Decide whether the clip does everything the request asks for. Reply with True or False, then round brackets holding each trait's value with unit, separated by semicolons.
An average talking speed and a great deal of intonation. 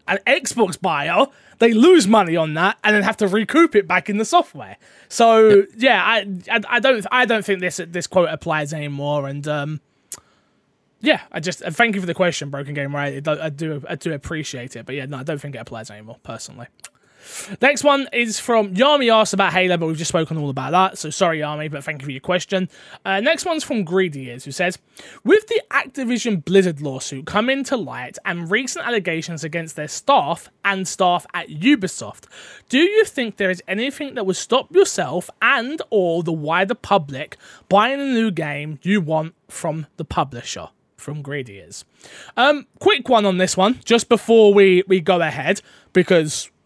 True (190 wpm; 6.6 semitones)